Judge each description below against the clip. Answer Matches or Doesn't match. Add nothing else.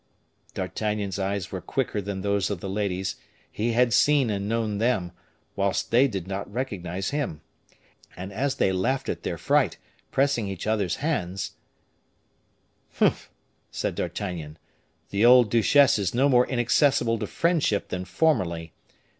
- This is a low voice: Matches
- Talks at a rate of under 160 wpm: Matches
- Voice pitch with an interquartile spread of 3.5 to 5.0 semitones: Matches